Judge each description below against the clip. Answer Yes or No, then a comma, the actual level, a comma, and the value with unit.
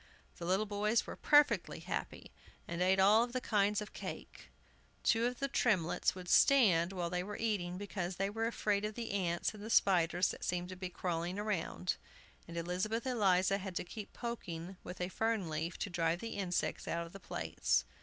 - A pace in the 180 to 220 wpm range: Yes, average, 195 wpm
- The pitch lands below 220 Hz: Yes, high, 190 Hz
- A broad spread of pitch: No, average, 3.4 semitones